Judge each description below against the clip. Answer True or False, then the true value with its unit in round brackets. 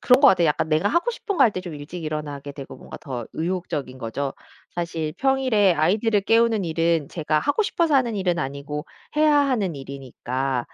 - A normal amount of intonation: False (7.7 semitones)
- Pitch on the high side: False (170 Hz)